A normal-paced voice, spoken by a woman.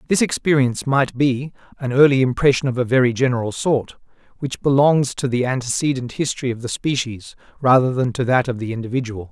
No: average, 180 wpm; male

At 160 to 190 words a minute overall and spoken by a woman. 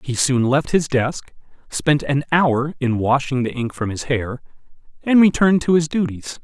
No: average, 185 wpm; male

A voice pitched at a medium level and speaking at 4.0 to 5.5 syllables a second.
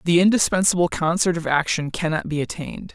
No: medium, 170 Hz; 6.1 syllables/s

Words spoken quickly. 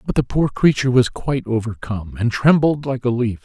Yes: fast, 210 wpm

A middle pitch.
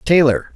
Yes: medium, 145 Hz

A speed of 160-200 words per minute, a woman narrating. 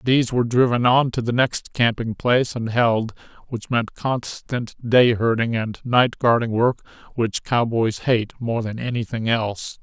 No: average, 165 wpm; male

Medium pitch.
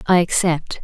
Yes: medium, 175 Hz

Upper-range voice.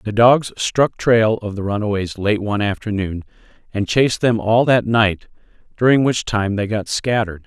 No: low, 110 Hz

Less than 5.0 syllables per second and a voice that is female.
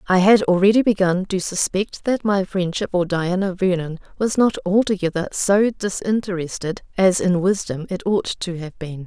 Yes: 4.7 syllables/s; female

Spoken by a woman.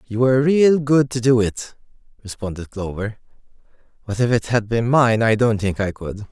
No: male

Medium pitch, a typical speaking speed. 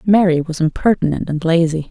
Yes: medium, 170 Hz; average, 160 wpm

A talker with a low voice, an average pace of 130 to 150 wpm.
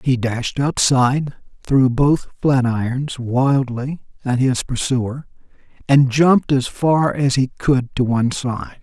Yes: low, 130 Hz; average, 145 wpm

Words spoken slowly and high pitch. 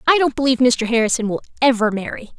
No: average, 200 wpm; high, 245 Hz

